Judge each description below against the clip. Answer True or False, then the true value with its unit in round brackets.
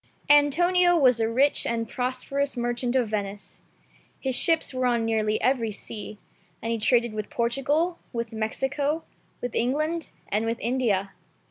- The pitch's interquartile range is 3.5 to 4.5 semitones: True (3.8 semitones)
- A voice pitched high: True (245 Hz)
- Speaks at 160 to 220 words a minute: False (145 wpm)